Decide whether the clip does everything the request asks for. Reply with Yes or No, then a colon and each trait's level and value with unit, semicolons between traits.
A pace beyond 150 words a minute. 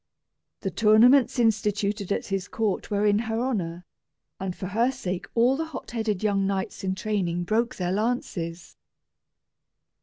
No: average, 145 wpm